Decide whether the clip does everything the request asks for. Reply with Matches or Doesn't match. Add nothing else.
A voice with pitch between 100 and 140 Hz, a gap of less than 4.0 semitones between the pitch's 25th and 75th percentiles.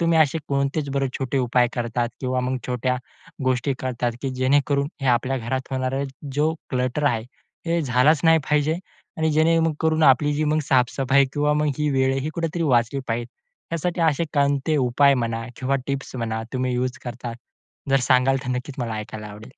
Matches